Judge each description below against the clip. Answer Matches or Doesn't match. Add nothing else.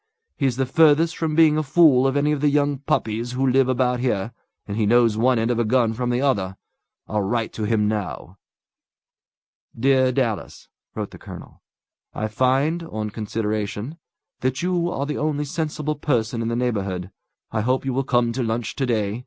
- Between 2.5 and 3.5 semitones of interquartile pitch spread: Doesn't match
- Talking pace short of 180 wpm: Doesn't match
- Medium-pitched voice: Doesn't match